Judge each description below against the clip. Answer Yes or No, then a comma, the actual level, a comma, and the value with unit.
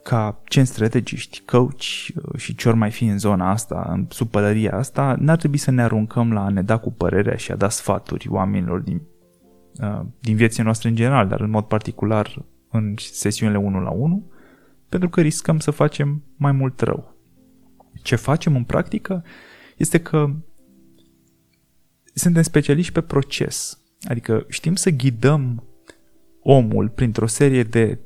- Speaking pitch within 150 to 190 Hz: No, low, 120 Hz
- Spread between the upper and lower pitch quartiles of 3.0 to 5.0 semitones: No, wide, 5.6 semitones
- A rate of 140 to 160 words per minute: Yes, average, 155 wpm